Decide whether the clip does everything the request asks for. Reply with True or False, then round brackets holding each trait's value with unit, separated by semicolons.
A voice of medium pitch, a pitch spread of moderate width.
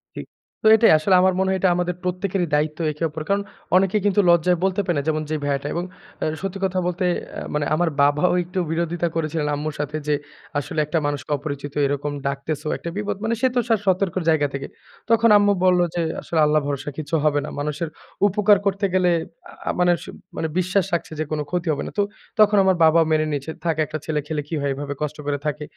True (165 Hz; 3.8 semitones)